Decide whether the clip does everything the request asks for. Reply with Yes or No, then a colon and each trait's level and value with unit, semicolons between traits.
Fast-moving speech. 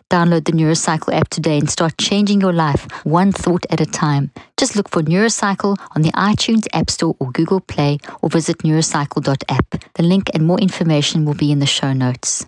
No: average, 195 wpm